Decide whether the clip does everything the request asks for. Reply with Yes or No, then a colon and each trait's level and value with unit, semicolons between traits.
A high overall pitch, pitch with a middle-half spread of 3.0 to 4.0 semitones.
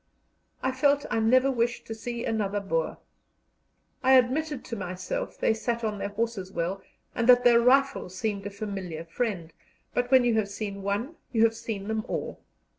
Yes: high, 225 Hz; average, 3.7 semitones